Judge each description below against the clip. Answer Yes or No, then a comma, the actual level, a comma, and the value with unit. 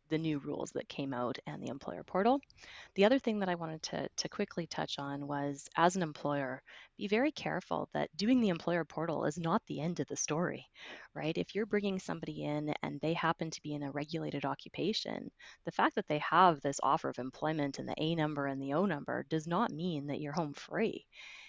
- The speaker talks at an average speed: No, fast, 220 wpm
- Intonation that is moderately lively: Yes, average, 3.6 semitones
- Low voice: No, medium, 160 Hz